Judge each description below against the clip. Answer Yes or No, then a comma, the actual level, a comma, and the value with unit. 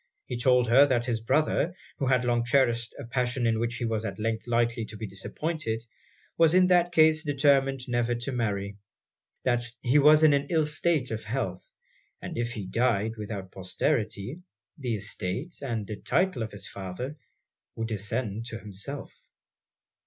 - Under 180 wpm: Yes, average, 165 wpm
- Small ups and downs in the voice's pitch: No, average, 4.1 semitones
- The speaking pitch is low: Yes, low, 120 Hz